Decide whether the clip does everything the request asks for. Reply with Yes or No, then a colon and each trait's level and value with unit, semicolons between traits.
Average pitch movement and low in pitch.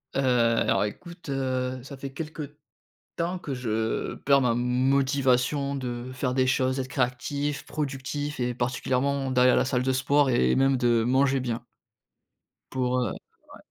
No: narrow, 2.0 semitones; low, 130 Hz